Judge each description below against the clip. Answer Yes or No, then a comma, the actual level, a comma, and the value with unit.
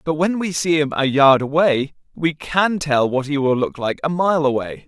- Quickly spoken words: Yes, fast, 235 wpm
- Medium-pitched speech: Yes, medium, 150 Hz